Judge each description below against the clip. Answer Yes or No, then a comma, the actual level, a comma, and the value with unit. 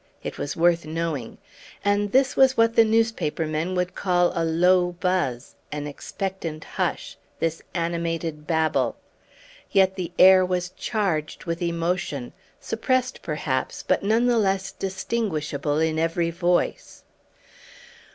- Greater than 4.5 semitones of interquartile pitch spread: No, average, 3.3 semitones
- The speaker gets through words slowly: Yes, slow, 130 wpm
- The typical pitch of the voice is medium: Yes, medium, 175 Hz